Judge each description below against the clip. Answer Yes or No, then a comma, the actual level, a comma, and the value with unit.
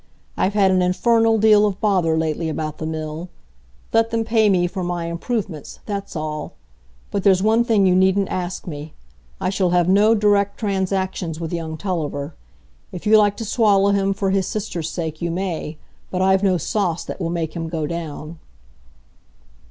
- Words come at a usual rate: Yes, average, 180 wpm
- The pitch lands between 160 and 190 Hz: Yes, medium, 185 Hz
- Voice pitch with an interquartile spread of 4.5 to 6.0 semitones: No, average, 3.5 semitones